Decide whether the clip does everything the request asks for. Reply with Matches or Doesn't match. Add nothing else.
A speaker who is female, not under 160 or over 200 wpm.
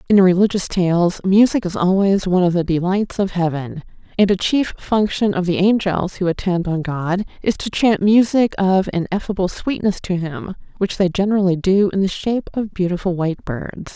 Matches